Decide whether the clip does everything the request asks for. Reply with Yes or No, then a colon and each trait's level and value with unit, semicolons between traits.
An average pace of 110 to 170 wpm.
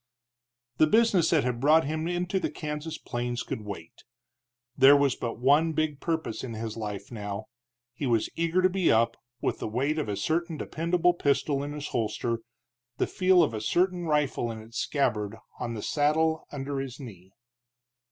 No: average, 180 wpm